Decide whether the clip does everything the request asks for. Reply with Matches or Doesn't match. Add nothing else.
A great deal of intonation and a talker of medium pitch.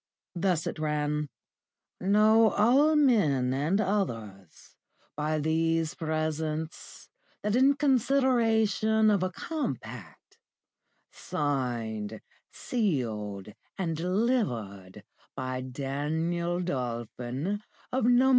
Matches